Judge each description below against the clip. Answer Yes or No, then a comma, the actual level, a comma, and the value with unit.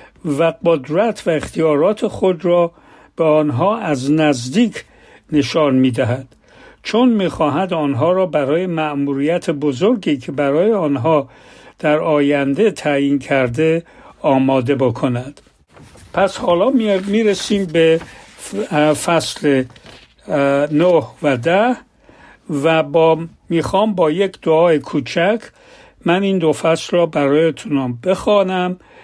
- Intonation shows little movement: No, average, 4.7 semitones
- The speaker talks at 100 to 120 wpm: Yes, average, 110 wpm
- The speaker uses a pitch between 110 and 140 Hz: No, medium, 160 Hz